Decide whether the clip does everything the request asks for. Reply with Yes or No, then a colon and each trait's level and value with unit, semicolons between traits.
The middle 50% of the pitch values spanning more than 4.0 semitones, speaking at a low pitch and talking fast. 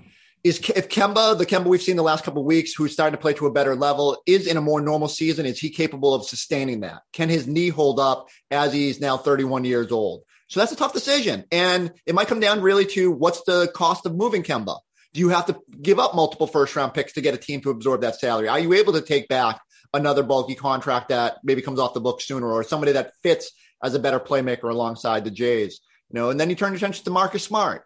No: average, 4.9 semitones; medium, 150 Hz; fast, 250 wpm